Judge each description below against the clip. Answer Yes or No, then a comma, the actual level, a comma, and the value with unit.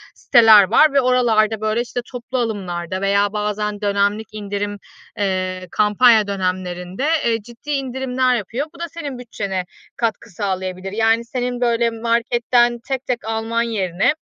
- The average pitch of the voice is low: No, high, 220 Hz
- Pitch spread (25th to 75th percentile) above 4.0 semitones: No, average, 3.2 semitones